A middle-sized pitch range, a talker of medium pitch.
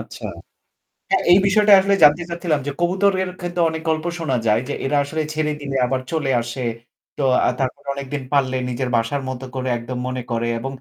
Yes: average, 4.8 semitones; medium, 145 Hz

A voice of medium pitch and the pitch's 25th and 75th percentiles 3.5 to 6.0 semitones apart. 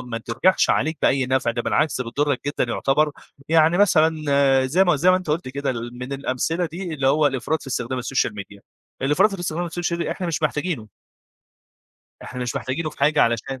Yes: medium, 145 Hz; average, 4.4 semitones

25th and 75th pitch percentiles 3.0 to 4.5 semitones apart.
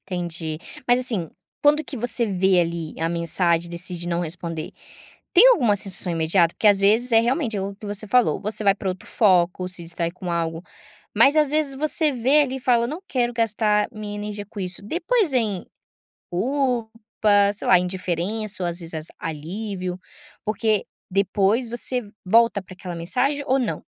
No: wide, 5.4 semitones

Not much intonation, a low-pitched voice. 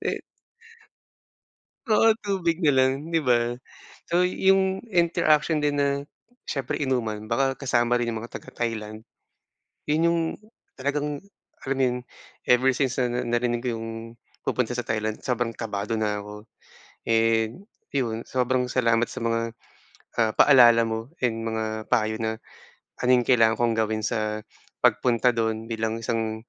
No: average, 3.0 semitones; low, 120 Hz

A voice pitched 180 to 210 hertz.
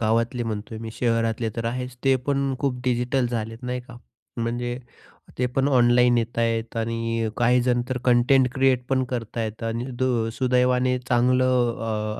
No: low, 120 Hz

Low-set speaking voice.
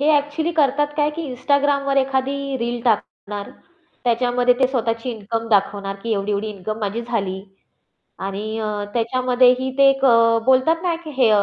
No: high, 245 Hz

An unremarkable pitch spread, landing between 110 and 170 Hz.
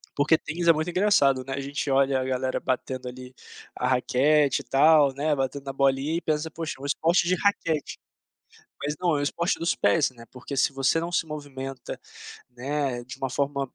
Yes: average, 3.0 semitones; medium, 140 Hz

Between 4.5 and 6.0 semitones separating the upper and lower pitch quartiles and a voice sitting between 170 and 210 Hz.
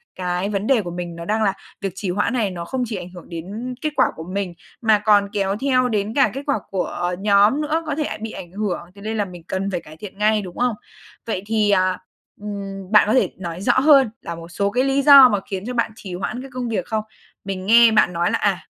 No: average, 3.9 semitones; high, 205 Hz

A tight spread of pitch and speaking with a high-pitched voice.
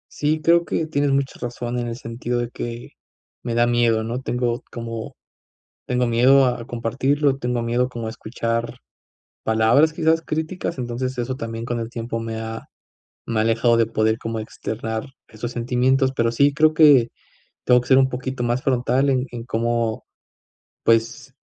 No: narrow, 2.3 semitones; low, 120 Hz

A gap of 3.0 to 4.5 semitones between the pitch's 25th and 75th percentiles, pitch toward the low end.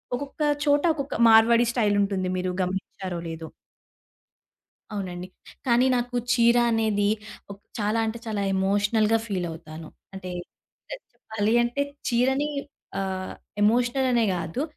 No: average, 4.1 semitones; high, 215 Hz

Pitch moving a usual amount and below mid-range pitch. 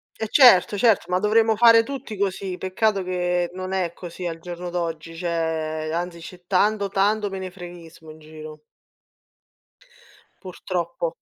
No: average, 3.0 semitones; medium, 180 Hz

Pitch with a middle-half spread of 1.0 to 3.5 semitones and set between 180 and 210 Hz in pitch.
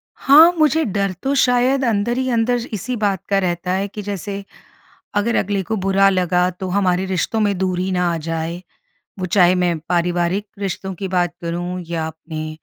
Yes: average, 2.9 semitones; high, 190 Hz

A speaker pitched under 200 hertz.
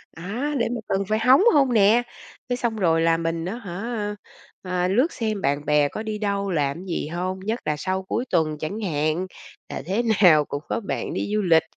Yes: high, 190 Hz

